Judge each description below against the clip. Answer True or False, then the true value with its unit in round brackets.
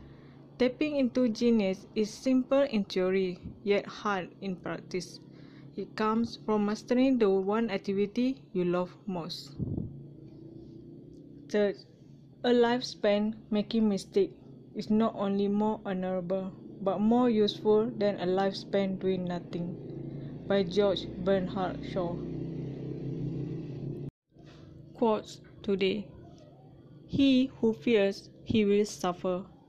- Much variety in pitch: False (4.8 semitones)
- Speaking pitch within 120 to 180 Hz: False (195 Hz)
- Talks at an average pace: False (105 wpm)